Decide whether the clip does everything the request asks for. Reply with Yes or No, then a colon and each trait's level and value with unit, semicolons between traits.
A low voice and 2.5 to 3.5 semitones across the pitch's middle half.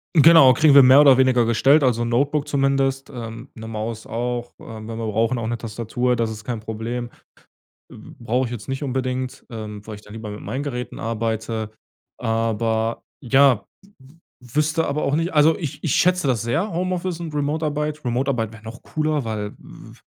No: low, 125 Hz; average, 4.1 semitones